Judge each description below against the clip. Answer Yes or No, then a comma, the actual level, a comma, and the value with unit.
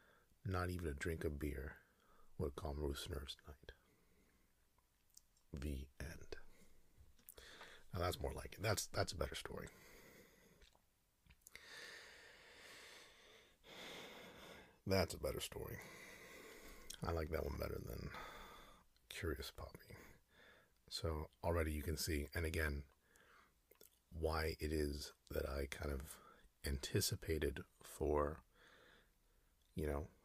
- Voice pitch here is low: Yes, very low, 80 Hz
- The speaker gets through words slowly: Yes, slow, 105 wpm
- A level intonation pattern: No, average, 3.5 semitones